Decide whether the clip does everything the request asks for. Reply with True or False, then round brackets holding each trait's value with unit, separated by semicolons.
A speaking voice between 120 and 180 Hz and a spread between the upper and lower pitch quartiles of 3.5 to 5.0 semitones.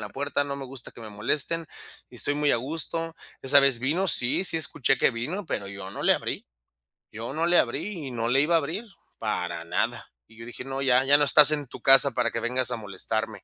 True (135 Hz; 4.3 semitones)